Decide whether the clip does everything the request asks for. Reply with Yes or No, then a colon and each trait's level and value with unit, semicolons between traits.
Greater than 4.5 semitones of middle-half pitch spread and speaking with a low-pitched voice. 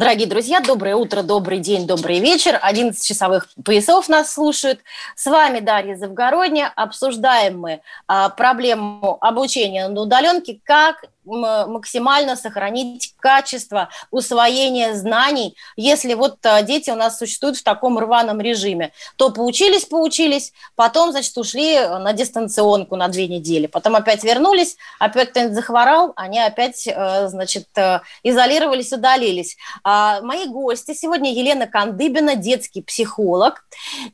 No: average, 4.9 semitones; high, 240 Hz